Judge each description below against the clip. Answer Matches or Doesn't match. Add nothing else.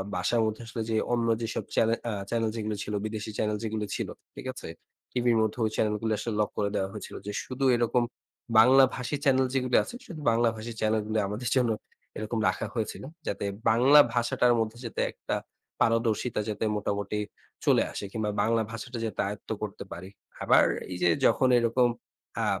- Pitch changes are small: Matches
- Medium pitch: Doesn't match